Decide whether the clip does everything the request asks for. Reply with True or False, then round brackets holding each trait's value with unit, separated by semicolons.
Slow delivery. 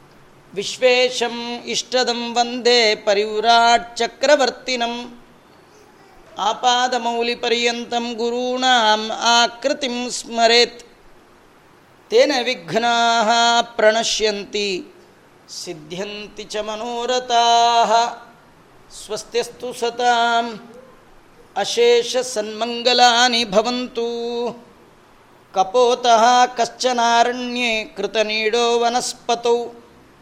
True (45 wpm)